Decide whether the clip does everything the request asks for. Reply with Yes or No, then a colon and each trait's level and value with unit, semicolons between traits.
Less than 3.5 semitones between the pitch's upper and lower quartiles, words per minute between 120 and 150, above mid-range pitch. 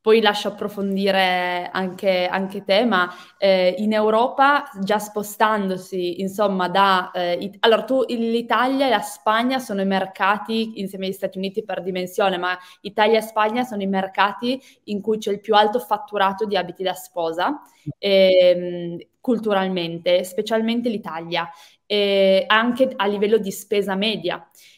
Yes: narrow, 2.6 semitones; average, 145 wpm; high, 200 Hz